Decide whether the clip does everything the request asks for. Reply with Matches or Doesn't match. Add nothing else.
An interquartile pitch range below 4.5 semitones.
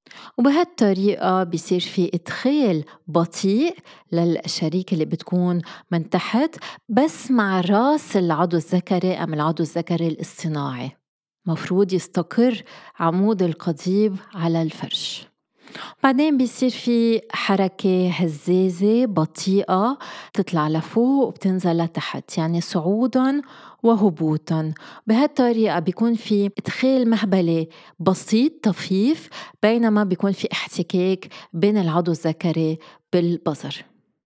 Doesn't match